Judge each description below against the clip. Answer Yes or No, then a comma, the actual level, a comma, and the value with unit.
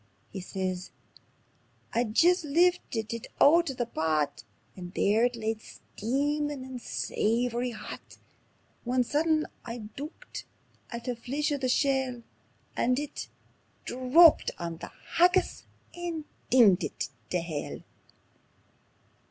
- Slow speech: Yes, slow, 125 wpm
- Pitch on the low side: No, very high, 250 Hz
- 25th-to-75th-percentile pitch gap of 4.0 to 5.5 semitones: Yes, average, 5.1 semitones